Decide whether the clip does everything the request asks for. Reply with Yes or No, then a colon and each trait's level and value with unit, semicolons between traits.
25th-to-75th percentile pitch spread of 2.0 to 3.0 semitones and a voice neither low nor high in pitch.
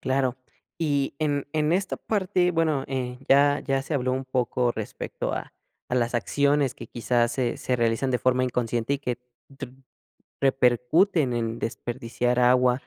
No: average, 2.7 semitones; low, 130 Hz